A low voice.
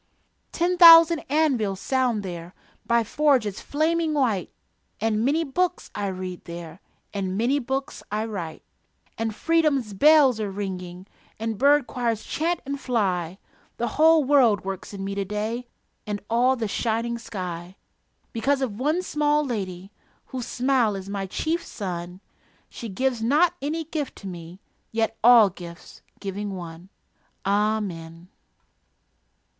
No: high, 225 Hz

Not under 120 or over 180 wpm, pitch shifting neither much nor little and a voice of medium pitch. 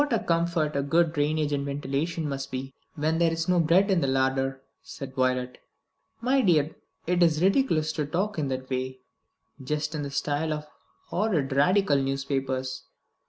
Yes: average, 165 wpm; average, 3.7 semitones; medium, 150 Hz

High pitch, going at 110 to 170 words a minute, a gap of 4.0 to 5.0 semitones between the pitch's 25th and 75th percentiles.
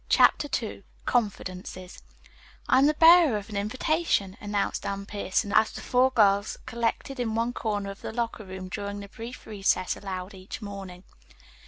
No: high, 205 Hz; average, 165 wpm; average, 3.3 semitones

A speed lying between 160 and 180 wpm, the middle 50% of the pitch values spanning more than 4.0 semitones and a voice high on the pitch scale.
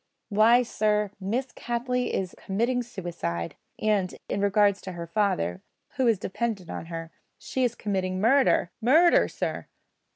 No: average, 140 wpm; average, 4.4 semitones; high, 210 Hz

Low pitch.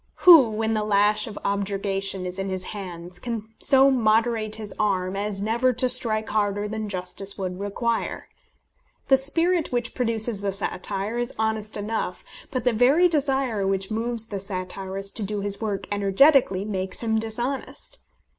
No: high, 215 Hz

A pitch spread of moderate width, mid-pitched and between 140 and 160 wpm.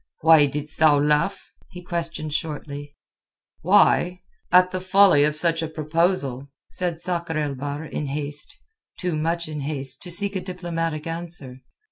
Yes: average, 3.1 semitones; medium, 160 Hz; average, 150 wpm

